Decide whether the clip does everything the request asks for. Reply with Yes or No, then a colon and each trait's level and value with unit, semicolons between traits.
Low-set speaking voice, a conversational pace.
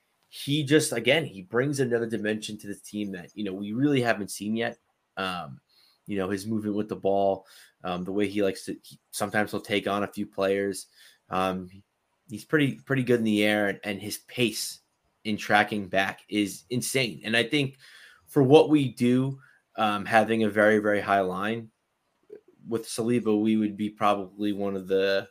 Yes: low, 105 Hz; average, 190 wpm